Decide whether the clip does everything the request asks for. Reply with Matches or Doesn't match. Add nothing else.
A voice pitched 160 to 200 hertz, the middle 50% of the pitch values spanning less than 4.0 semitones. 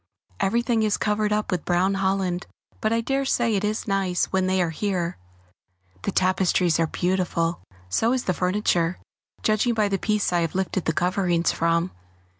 Matches